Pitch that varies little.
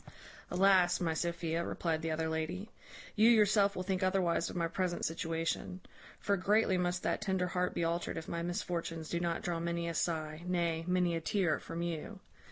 Yes: narrow, 2.0 semitones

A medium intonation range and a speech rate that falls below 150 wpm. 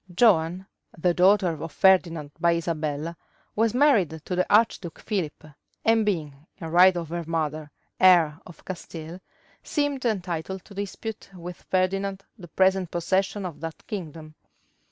Yes: average, 3.1 semitones; average, 140 wpm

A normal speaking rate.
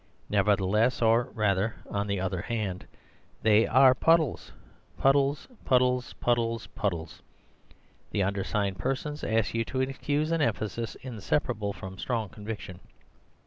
No: slow, 115 wpm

